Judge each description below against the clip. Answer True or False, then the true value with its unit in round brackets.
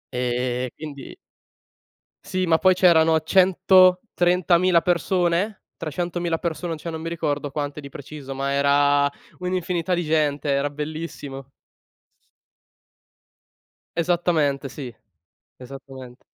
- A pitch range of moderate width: True (3.8 semitones)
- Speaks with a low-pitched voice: False (160 Hz)